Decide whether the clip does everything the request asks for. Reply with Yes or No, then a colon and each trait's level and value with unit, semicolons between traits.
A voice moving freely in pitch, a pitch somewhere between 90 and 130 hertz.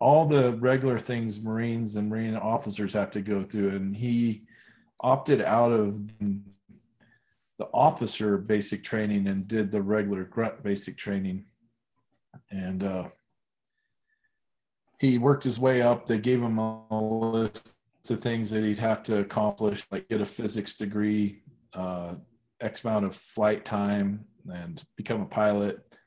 No: narrow, 2.5 semitones; low, 110 Hz